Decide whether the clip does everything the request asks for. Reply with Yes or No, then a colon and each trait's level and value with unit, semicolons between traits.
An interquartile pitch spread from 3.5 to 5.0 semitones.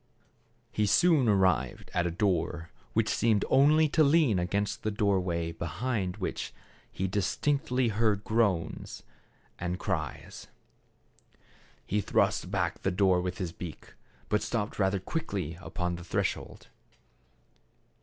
Yes: average, 3.8 semitones